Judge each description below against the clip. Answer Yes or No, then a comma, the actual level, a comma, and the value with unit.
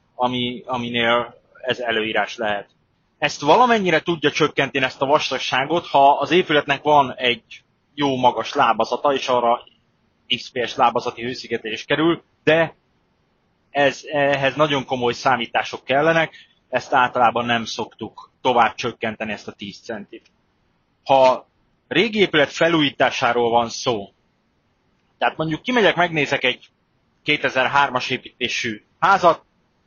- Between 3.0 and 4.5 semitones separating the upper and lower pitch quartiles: Yes, average, 3.6 semitones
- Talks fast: No, average, 115 wpm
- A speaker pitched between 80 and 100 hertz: No, low, 135 Hz